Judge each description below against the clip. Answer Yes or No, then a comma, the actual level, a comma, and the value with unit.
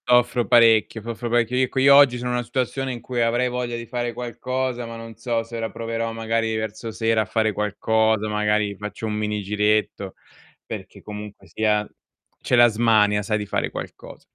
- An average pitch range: No, narrow, 2.1 semitones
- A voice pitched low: Yes, low, 115 Hz